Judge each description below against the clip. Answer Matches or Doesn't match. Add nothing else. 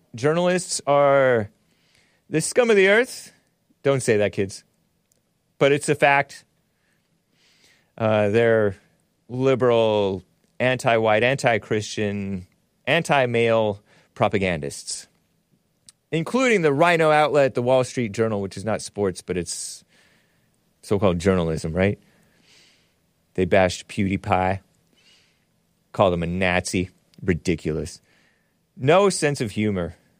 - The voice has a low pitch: Matches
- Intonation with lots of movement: Matches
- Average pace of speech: Doesn't match